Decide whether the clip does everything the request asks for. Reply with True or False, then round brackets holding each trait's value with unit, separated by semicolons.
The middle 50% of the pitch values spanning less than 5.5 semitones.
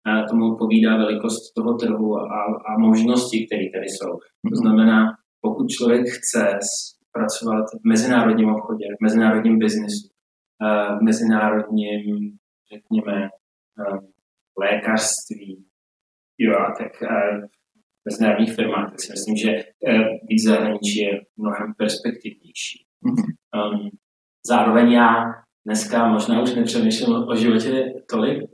True (2.4 semitones)